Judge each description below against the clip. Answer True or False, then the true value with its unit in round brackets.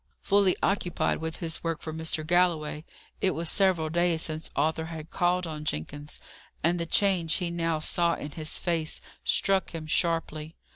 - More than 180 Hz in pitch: False (165 Hz)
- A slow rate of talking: False (165 wpm)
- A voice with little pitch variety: True (2.0 semitones)